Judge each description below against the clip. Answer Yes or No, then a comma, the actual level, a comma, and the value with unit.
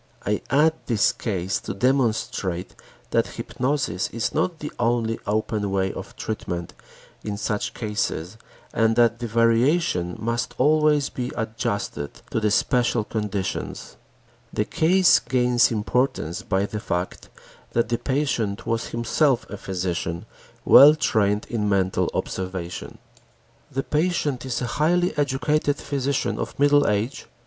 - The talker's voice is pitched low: Yes, low, 115 Hz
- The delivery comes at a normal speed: No, slow, 130 wpm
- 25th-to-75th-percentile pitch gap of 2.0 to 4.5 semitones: No, average, 5.1 semitones